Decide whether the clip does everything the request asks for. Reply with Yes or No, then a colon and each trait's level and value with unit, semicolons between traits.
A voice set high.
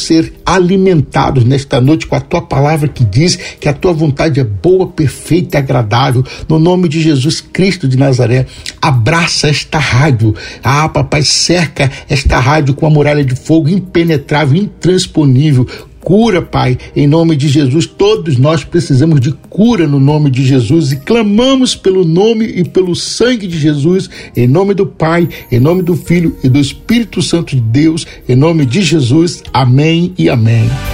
No: medium, 155 Hz